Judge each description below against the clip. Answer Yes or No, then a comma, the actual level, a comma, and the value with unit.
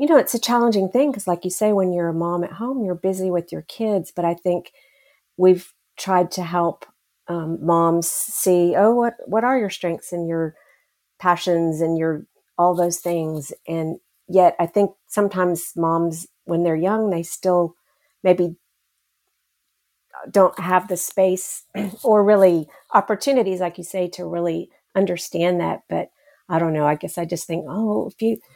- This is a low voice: No, medium, 180 Hz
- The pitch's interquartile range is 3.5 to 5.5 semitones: No, average, 3.0 semitones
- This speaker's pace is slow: No, average, 175 wpm